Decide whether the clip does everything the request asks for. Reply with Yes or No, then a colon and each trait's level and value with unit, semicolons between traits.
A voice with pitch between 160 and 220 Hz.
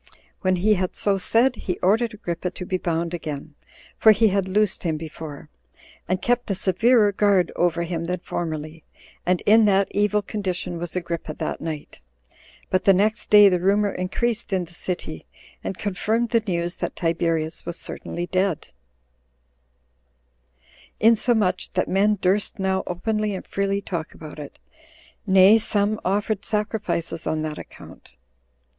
Yes: medium, 185 Hz